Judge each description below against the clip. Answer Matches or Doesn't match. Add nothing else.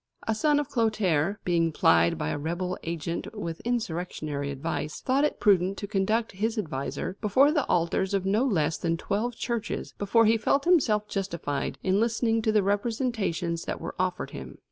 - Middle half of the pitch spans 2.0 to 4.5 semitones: Doesn't match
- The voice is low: Doesn't match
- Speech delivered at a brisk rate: Doesn't match